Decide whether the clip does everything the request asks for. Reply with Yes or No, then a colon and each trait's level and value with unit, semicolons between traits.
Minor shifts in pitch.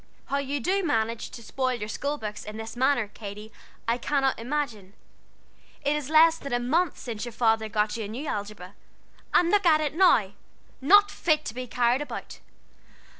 No: average, 5.2 semitones